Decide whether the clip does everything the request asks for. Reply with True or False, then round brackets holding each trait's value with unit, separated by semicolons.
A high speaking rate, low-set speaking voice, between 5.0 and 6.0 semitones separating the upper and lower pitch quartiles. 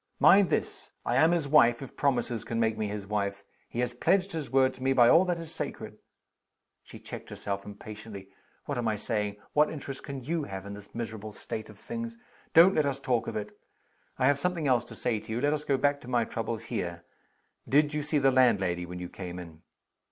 True (225 wpm; 120 Hz; 5.5 semitones)